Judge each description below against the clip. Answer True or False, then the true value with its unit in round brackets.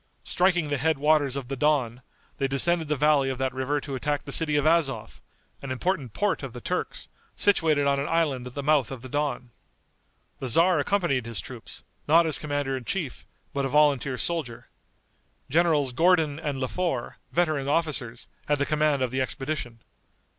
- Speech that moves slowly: False (185 wpm)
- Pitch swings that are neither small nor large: True (3.0 semitones)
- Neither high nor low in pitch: True (145 Hz)